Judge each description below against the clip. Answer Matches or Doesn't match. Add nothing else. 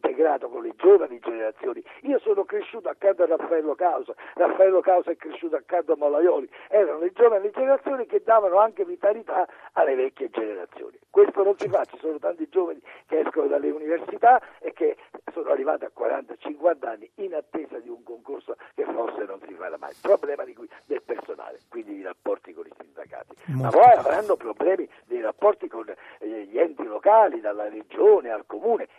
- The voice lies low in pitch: Doesn't match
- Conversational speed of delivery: Doesn't match